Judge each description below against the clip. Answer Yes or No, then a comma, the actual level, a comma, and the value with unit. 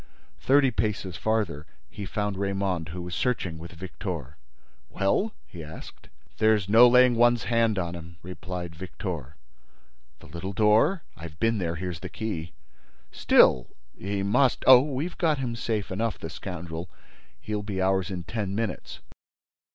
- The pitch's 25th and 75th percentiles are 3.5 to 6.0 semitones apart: Yes, average, 4.8 semitones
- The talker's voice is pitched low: Yes, very low, 95 Hz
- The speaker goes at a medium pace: Yes, average, 145 wpm